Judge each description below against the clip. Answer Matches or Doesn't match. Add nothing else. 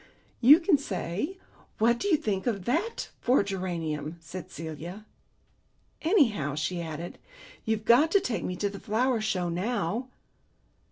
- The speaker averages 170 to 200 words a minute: Doesn't match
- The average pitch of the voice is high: Matches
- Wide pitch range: Matches